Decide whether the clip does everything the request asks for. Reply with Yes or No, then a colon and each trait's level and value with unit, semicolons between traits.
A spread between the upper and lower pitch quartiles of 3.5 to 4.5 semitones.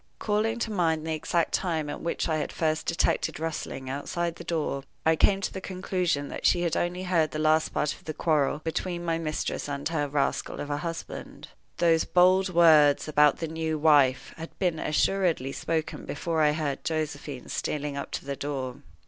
No: average, 2.7 semitones